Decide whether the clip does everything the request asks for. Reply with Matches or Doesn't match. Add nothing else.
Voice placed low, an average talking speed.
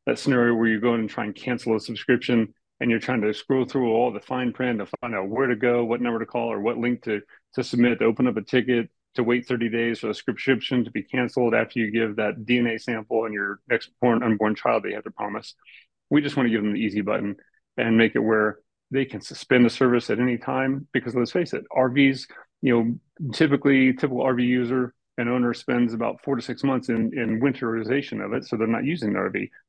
Doesn't match